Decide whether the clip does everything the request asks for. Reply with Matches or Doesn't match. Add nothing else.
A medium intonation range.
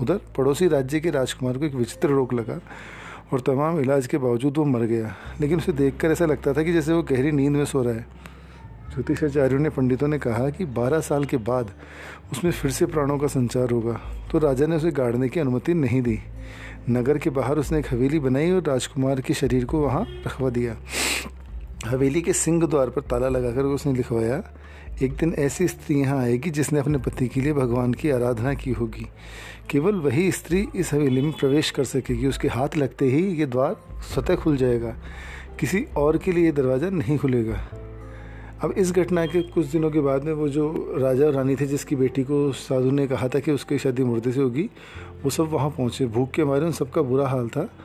Matches